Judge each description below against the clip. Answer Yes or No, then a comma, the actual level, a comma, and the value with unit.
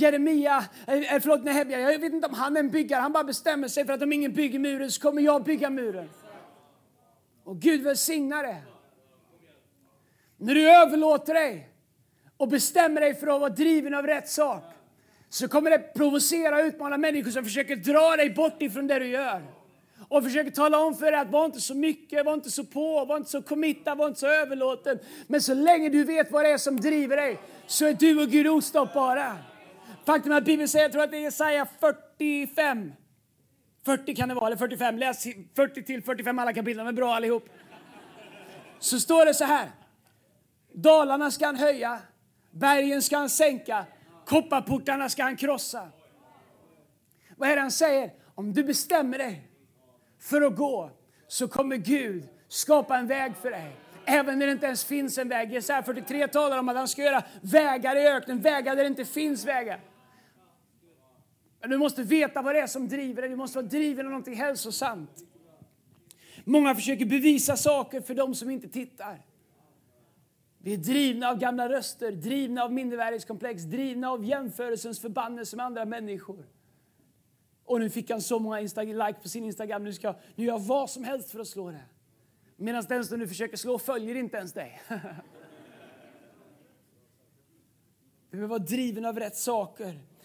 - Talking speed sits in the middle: Yes, average, 175 wpm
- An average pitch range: Yes, average, 4.6 semitones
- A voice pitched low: No, very high, 265 Hz